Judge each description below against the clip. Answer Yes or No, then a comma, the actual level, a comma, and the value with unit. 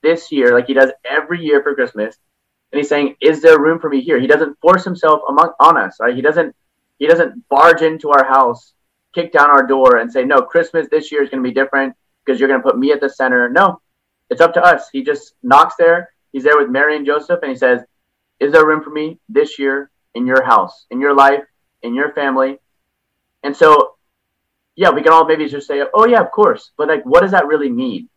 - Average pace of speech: No, fast, 240 wpm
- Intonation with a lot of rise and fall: No, average, 3.7 semitones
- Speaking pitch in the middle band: Yes, medium, 150 Hz